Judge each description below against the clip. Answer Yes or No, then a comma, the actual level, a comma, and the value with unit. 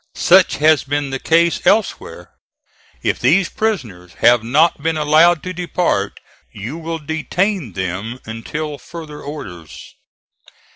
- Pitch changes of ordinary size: No, wide, 6.2 semitones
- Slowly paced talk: Yes, slow, 125 wpm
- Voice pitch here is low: No, medium, 150 Hz